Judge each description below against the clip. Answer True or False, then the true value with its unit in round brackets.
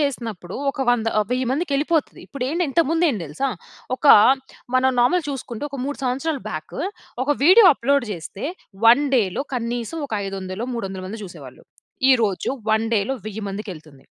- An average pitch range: False (6.0 semitones)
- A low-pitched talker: False (245 Hz)